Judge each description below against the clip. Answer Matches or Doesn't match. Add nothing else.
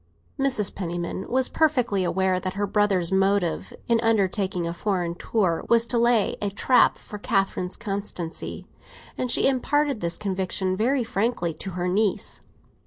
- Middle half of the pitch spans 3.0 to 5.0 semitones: Matches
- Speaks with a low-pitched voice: Doesn't match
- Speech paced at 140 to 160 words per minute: Matches